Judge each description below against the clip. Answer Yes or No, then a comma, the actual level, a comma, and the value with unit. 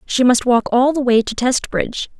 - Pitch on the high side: Yes, high, 245 Hz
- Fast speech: Yes, fast, 220 wpm